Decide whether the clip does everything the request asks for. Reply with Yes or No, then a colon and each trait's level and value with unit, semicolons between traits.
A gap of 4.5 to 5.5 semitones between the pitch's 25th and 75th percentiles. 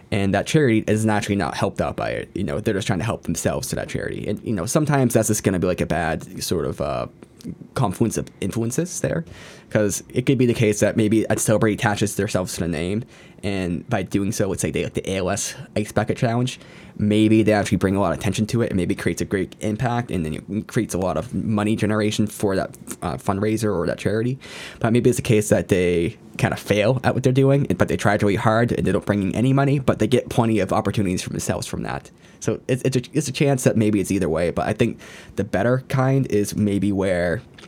No: average, 3.1 semitones